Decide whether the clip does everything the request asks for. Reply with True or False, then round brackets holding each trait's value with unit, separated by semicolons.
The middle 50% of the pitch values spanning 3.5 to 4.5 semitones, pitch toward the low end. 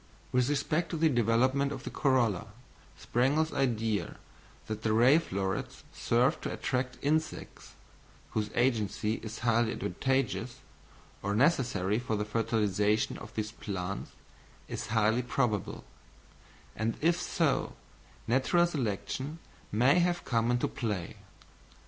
True (4.0 semitones; 120 Hz)